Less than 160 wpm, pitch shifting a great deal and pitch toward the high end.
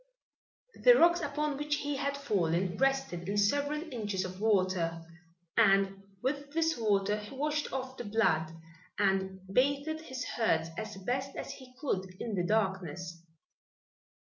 Yes: average, 140 wpm; wide, 6.8 semitones; high, 220 Hz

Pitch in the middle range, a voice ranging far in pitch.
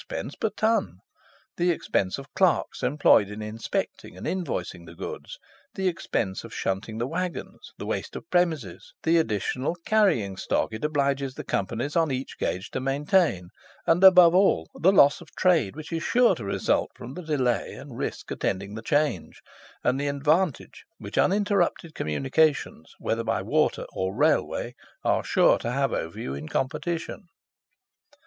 Yes: medium, 145 Hz; wide, 7.5 semitones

